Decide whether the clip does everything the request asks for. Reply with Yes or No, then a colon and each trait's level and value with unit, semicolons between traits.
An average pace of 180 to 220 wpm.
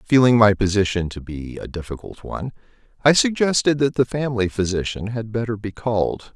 No: average, 170 wpm